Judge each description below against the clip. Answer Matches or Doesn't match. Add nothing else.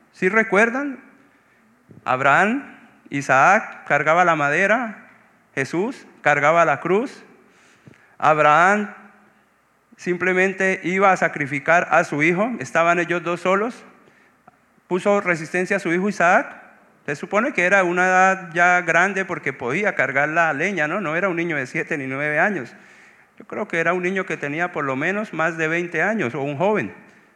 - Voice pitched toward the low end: Doesn't match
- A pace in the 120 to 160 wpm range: Matches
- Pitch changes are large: Doesn't match